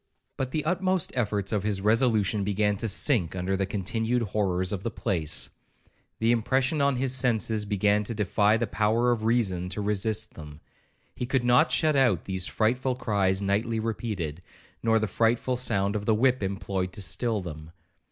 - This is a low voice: Yes, low, 110 Hz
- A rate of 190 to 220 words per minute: No, average, 175 wpm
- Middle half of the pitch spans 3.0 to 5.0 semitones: Yes, average, 3.7 semitones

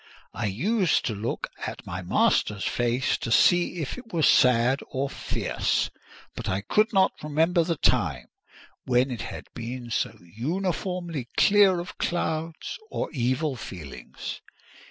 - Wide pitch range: Yes, wide, 6.9 semitones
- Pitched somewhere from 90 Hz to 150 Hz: Yes, medium, 140 Hz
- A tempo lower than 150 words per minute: Yes, average, 140 wpm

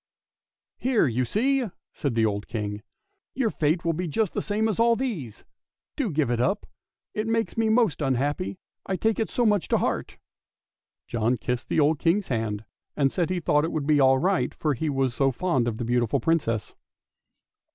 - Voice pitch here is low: No, medium, 155 Hz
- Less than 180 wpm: No, fast, 205 wpm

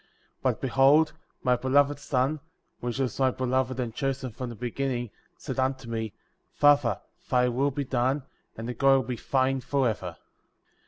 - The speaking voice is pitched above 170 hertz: No, low, 130 Hz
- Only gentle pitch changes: Yes, narrow, 1.9 semitones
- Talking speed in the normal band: Yes, average, 170 wpm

